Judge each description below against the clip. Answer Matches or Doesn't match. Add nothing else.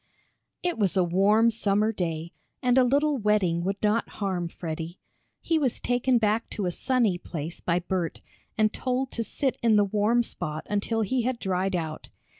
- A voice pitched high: Matches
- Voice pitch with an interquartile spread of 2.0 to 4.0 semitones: Doesn't match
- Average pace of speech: Matches